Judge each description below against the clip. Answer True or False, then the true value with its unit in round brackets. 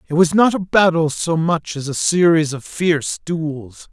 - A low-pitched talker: False (160 Hz)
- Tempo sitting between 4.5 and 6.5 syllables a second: False (4.3 syllables/s)